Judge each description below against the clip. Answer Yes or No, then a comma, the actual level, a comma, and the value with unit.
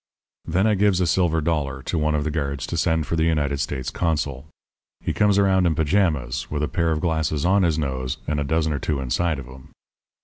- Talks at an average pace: No, fast, 230 wpm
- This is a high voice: No, very low, 80 Hz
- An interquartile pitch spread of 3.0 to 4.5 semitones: Yes, average, 3.3 semitones